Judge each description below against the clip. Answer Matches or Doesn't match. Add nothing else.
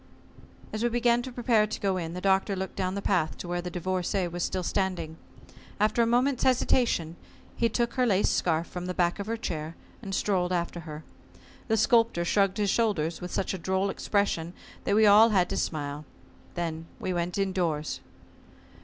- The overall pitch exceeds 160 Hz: Matches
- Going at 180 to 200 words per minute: Matches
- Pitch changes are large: Doesn't match